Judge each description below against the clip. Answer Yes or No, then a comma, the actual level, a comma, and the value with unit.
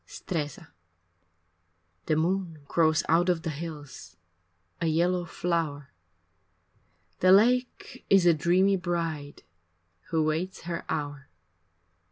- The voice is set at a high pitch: No, medium, 165 Hz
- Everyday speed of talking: No, slow, 110 wpm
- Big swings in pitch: No, average, 2.7 semitones